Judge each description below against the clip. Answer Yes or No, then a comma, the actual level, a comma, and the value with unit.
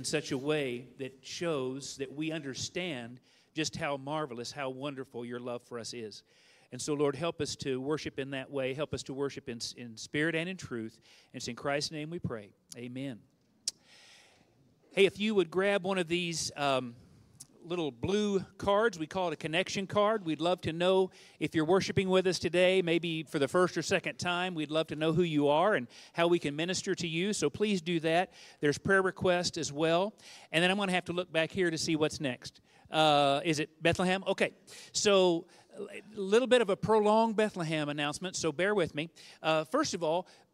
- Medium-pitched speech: Yes, medium, 160 Hz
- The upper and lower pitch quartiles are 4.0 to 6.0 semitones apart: Yes, average, 4.7 semitones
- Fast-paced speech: Yes, fast, 210 wpm